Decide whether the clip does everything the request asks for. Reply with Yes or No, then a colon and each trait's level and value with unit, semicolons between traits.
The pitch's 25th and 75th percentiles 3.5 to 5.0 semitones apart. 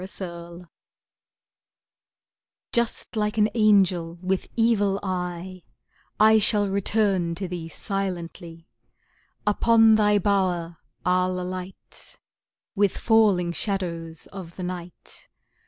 No: average, 2.9 semitones